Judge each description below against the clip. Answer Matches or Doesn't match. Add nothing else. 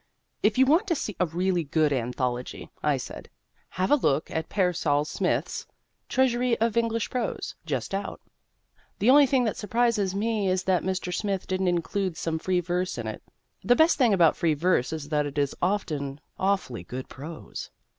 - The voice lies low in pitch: Doesn't match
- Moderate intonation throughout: Doesn't match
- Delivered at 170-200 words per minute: Matches